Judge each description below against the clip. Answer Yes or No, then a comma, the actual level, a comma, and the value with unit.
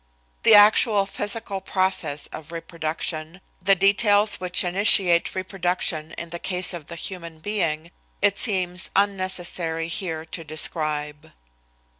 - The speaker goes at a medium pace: No, slow, 120 wpm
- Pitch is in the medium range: Yes, medium, 180 Hz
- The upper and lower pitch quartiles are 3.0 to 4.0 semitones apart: Yes, average, 3.3 semitones